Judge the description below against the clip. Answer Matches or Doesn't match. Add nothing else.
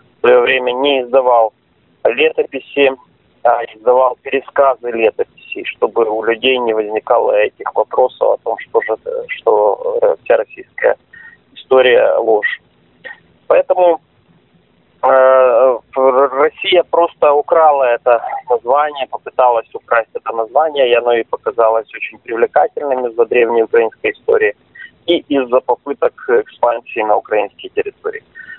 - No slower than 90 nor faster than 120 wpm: Matches